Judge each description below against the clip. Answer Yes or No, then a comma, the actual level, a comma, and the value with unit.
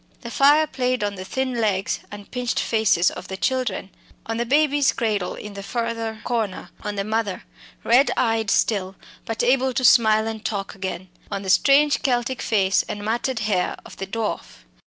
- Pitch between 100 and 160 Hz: No, high, 225 Hz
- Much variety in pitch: No, average, 3.8 semitones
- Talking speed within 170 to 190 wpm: Yes, average, 180 wpm